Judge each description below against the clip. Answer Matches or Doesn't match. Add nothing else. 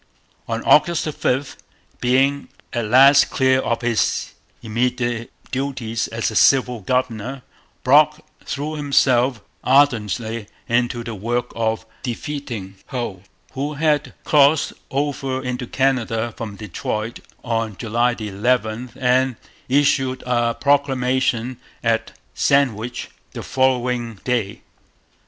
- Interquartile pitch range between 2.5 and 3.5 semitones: Matches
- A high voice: Doesn't match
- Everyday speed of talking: Doesn't match